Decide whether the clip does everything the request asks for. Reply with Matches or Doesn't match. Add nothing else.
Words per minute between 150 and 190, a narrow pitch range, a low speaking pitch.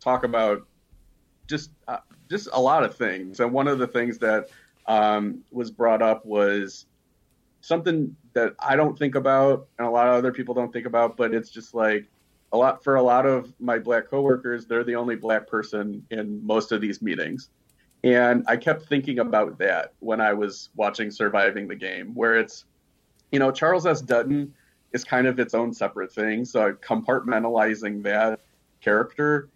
Doesn't match